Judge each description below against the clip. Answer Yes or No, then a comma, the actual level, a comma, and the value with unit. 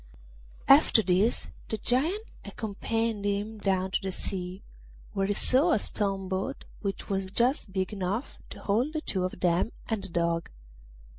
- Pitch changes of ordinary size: Yes, average, 3.2 semitones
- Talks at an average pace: Yes, average, 160 wpm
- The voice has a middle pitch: No, high, 200 Hz